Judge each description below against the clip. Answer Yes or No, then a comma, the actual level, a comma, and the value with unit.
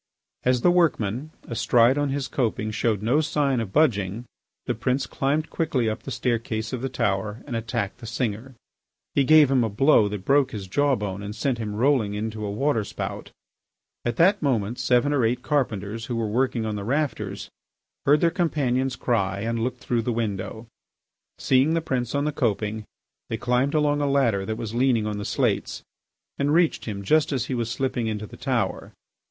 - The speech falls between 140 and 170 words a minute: No, average, 190 wpm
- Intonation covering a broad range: No, average, 4.1 semitones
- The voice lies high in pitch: No, low, 120 Hz